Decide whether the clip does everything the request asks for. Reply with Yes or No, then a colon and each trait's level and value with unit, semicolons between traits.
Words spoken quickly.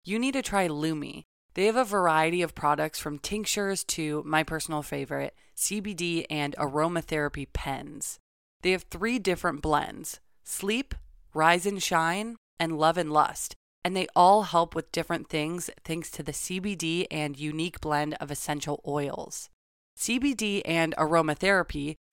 No: average, 145 wpm